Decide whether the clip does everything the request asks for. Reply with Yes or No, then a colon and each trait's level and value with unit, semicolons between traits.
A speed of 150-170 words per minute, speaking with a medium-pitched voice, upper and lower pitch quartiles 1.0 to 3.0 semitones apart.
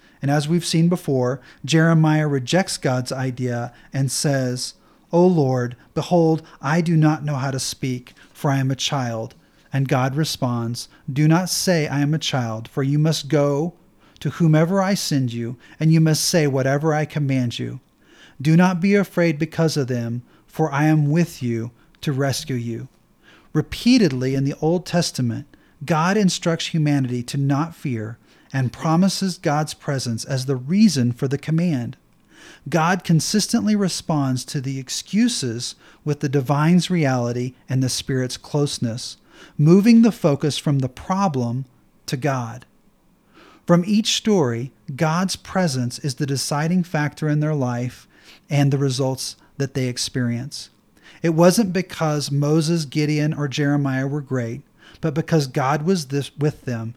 No: average, 155 wpm; medium, 145 Hz; average, 4.0 semitones